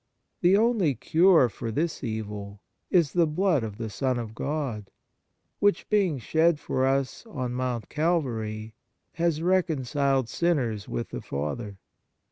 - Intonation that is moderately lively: No, wide, 7.1 semitones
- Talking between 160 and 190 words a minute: No, slow, 135 wpm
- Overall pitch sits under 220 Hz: Yes, low, 135 Hz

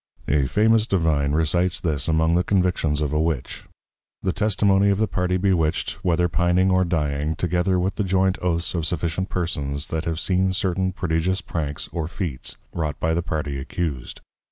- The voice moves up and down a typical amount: Yes, average, 3.0 semitones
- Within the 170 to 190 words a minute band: Yes, average, 175 wpm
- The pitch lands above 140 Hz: No, very low, 85 Hz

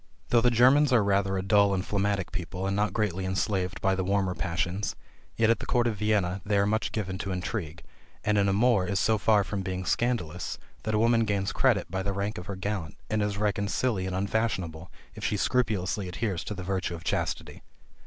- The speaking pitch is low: Yes, low, 100 Hz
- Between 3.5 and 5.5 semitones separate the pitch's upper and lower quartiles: No, narrow, 2.4 semitones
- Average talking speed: No, fast, 215 wpm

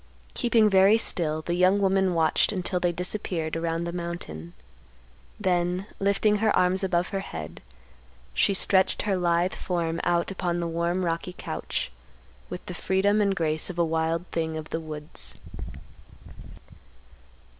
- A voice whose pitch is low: No, medium, 175 Hz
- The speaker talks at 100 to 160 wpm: Yes, average, 145 wpm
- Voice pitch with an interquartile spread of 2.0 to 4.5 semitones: Yes, narrow, 2.6 semitones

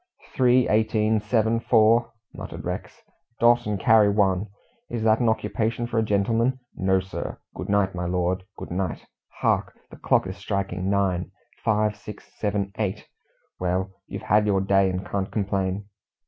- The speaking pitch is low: Yes, low, 105 Hz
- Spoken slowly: No, average, 160 wpm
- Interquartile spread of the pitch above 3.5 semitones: No, average, 2.7 semitones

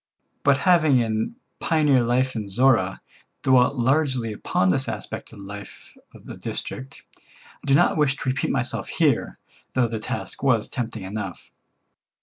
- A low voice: Yes, low, 125 Hz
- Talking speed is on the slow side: No, average, 160 wpm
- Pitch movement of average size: Yes, average, 4.0 semitones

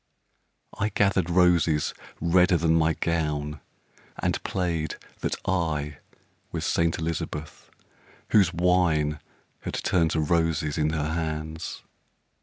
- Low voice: Yes, very low, 80 Hz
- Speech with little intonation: Yes, narrow, 2.3 semitones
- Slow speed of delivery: Yes, slow, 110 wpm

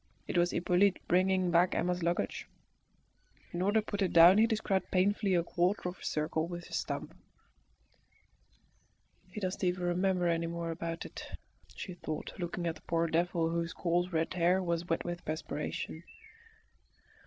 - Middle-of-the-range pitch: Yes, medium, 175 Hz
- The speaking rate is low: No, average, 165 wpm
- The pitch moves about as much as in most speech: No, narrow, 1.7 semitones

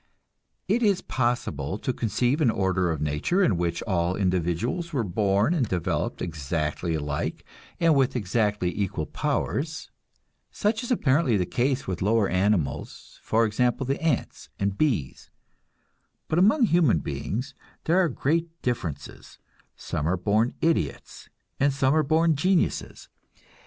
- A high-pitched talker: No, low, 115 Hz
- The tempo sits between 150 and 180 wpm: No, average, 140 wpm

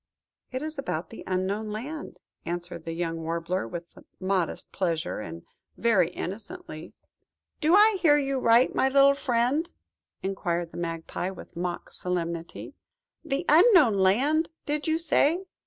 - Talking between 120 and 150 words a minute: Yes, slow, 135 wpm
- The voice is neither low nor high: No, high, 215 Hz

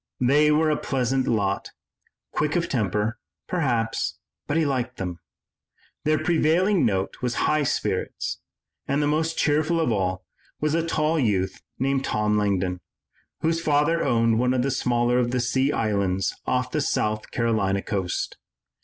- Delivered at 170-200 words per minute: No, average, 155 wpm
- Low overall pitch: Yes, low, 125 Hz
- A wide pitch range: Yes, wide, 6.0 semitones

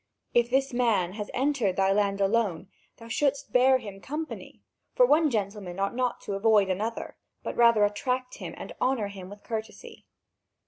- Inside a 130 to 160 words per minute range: No, average, 170 wpm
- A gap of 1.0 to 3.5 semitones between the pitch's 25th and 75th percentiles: No, average, 4.3 semitones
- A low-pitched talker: No, high, 220 Hz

